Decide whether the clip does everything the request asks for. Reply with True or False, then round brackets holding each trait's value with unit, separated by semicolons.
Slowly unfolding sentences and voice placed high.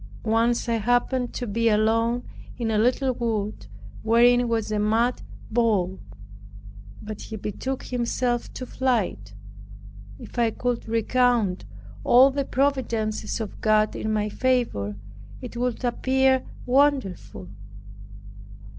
True (120 wpm; 235 Hz)